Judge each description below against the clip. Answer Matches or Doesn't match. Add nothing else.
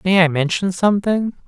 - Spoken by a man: Matches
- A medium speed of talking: Matches